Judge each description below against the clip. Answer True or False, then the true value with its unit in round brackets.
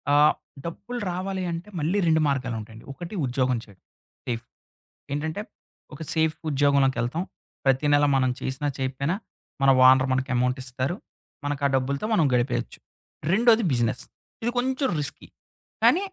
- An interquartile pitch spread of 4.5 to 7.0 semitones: True (4.8 semitones)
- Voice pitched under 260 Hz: True (140 Hz)